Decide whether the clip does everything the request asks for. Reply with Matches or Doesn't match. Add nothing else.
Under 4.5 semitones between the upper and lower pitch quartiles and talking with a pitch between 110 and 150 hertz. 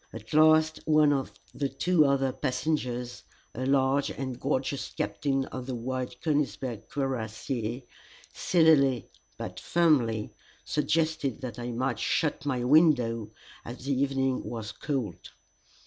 Matches